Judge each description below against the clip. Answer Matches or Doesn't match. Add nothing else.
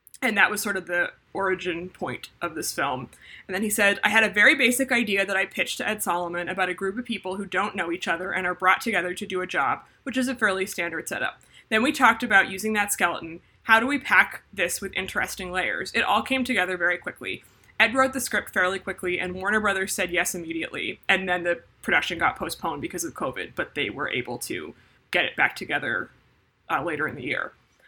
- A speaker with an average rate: Doesn't match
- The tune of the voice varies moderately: Matches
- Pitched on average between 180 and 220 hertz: Matches